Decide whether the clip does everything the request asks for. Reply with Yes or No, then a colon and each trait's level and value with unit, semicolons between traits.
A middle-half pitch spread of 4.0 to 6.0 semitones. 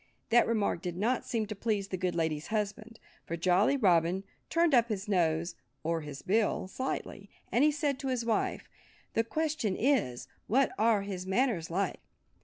Yes: average, 5.1 semitones